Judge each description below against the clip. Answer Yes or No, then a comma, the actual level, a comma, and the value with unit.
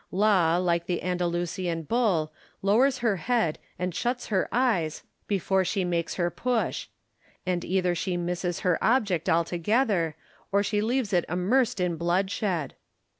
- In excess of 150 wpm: No, average, 140 wpm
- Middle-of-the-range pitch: Yes, medium, 180 Hz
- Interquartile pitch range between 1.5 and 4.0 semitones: Yes, average, 3.7 semitones